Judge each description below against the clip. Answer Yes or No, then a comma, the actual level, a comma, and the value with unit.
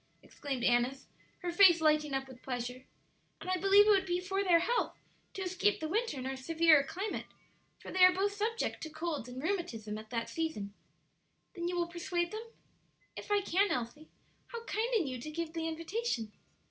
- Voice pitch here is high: Yes, very high, 335 Hz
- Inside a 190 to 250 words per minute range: Yes, average, 195 wpm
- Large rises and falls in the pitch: Yes, wide, 6.3 semitones